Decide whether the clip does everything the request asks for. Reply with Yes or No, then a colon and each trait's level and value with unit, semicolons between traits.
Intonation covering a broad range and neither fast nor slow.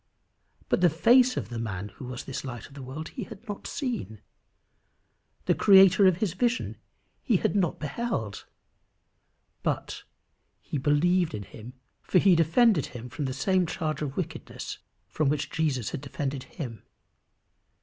Yes: wide, 6.7 semitones; average, 160 wpm